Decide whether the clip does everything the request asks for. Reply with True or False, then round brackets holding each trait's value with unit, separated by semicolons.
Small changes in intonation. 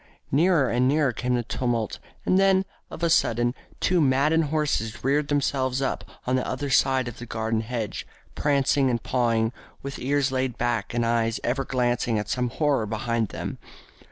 False (3.2 semitones)